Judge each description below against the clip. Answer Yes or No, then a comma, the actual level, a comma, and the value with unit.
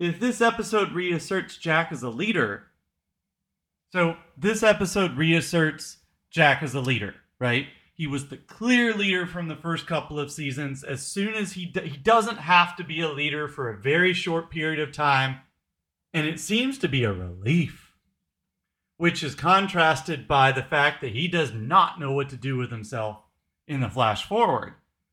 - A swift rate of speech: No, average, 175 wpm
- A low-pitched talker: No, medium, 155 Hz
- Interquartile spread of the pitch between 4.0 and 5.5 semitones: Yes, average, 4.9 semitones